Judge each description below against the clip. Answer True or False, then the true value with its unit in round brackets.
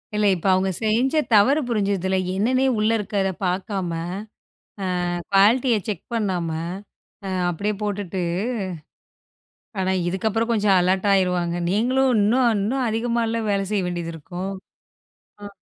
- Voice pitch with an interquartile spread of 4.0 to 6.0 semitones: False (3.3 semitones)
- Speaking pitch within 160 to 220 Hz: True (205 Hz)